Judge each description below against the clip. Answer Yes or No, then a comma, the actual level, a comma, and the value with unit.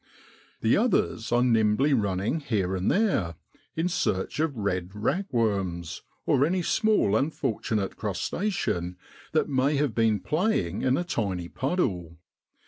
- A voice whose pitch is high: No, low, 115 Hz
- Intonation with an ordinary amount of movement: No, wide, 8.3 semitones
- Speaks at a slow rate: Yes, slow, 130 wpm